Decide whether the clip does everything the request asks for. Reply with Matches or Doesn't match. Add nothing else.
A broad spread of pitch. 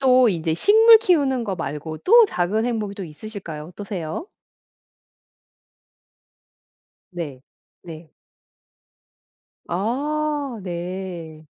Matches